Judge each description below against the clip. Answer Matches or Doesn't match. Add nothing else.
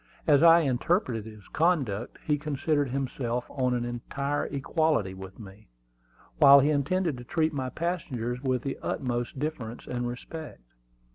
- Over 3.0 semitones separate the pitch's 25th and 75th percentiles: Matches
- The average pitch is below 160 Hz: Matches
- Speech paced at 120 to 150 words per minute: Matches